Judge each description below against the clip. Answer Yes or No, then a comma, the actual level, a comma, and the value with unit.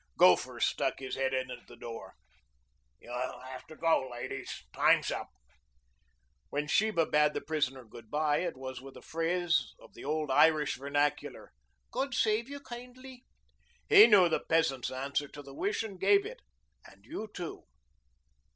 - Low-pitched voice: No, medium, 150 Hz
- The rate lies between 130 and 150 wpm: No, average, 160 wpm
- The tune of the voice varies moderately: No, wide, 7.5 semitones